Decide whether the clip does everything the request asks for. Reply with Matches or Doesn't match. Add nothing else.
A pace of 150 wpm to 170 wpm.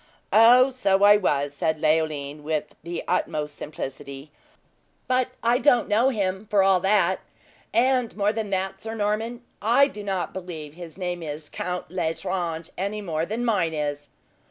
Matches